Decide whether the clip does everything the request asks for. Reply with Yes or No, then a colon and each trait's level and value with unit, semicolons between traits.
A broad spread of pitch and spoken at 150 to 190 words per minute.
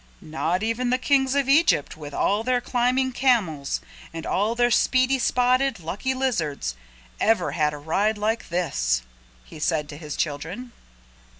Yes: wide, 8.3 semitones; average, 155 wpm